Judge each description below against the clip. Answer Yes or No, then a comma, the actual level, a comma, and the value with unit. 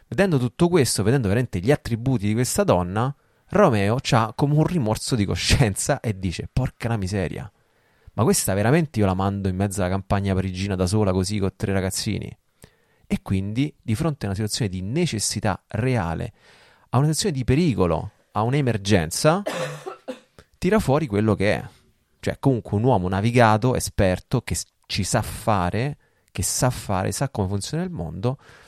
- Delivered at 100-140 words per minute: No, average, 165 wpm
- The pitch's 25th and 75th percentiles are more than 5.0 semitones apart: Yes, wide, 5.6 semitones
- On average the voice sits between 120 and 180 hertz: No, low, 110 Hz